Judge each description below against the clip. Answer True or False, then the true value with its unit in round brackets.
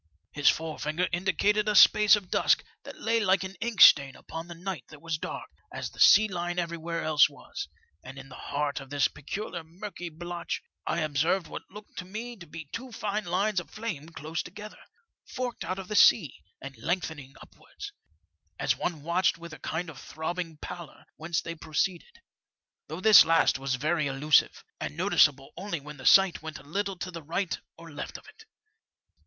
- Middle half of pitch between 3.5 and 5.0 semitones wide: True (4.1 semitones)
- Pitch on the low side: False (170 Hz)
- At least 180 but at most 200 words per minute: True (190 wpm)